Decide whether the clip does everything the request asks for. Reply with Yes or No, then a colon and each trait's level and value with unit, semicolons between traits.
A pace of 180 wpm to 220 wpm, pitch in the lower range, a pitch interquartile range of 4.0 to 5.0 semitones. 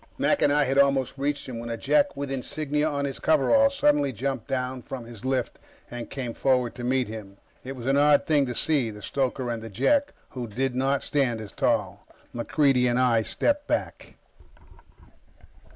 No: average, 190 wpm; low, 130 Hz; average, 2.9 semitones